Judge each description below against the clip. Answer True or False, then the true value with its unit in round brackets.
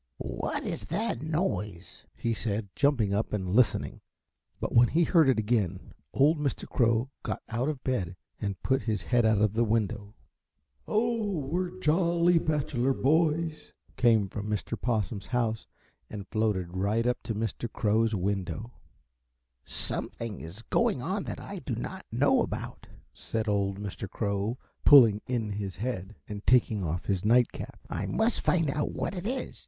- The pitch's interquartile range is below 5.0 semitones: False (5.4 semitones)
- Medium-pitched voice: False (115 Hz)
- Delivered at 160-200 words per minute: True (165 wpm)